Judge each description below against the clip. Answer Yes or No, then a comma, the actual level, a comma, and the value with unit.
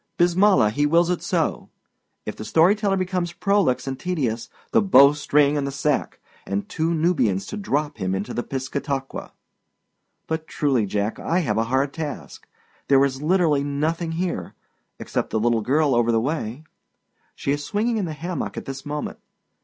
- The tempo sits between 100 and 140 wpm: No, average, 175 wpm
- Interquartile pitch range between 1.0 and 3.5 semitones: No, average, 4.6 semitones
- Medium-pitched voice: Yes, medium, 145 Hz